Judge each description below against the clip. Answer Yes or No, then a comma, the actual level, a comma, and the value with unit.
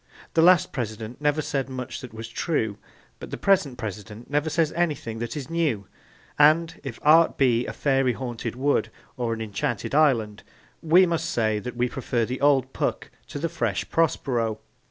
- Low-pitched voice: Yes, low, 130 Hz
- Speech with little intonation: No, average, 5.0 semitones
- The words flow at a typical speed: Yes, average, 175 wpm